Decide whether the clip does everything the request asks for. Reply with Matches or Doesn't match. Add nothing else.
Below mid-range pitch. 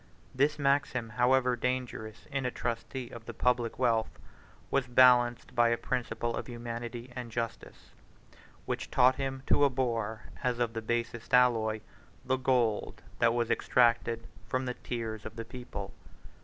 Matches